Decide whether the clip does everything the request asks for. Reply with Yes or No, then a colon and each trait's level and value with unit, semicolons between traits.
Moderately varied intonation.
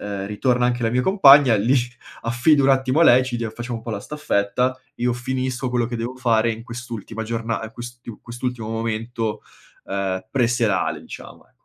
No: narrow, 2.1 semitones